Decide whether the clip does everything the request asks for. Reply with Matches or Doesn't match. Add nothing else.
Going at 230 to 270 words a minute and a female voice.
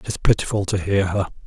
Doesn't match